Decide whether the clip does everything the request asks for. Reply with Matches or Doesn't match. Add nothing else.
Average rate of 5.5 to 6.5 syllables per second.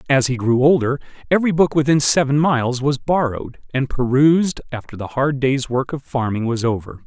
Matches